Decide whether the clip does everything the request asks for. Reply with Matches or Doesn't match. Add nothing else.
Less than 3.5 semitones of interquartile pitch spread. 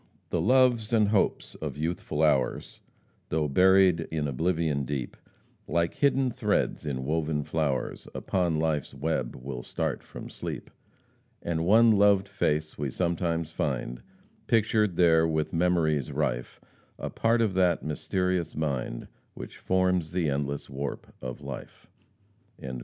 Doesn't match